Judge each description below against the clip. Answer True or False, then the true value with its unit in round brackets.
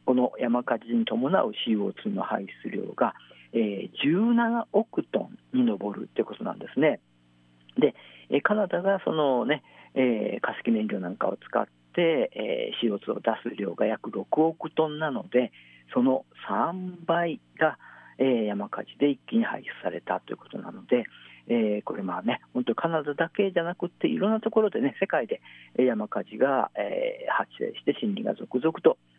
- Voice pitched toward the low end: False (165 Hz)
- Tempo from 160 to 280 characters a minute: True (270 characters per minute)